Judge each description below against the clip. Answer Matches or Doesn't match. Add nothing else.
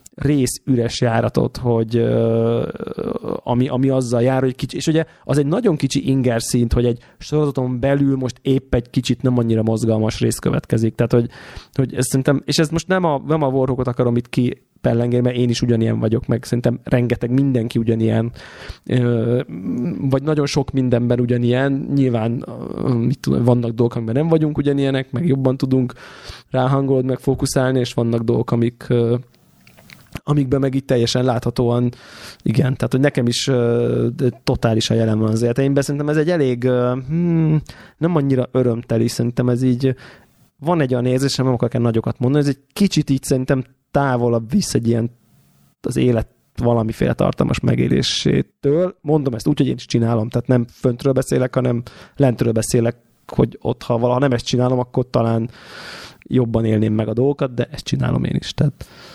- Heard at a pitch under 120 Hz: Doesn't match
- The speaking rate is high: Matches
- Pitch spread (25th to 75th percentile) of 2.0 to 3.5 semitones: Matches